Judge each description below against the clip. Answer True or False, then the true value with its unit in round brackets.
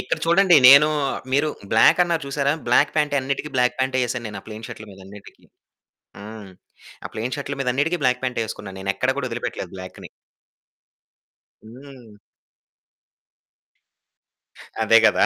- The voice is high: False (125 Hz)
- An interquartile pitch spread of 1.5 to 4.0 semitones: False (4.5 semitones)